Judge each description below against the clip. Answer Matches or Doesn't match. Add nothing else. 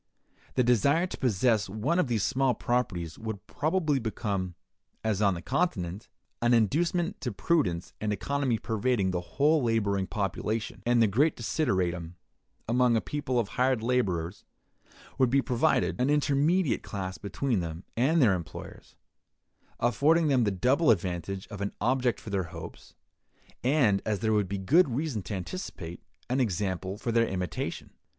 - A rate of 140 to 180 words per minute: Matches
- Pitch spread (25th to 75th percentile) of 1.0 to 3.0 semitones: Doesn't match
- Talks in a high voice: Doesn't match